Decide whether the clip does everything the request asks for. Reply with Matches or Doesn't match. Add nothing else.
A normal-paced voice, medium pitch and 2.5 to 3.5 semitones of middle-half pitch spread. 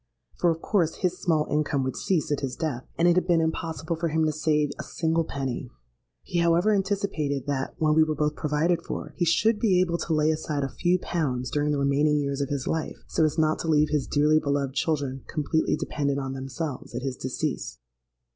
Doesn't match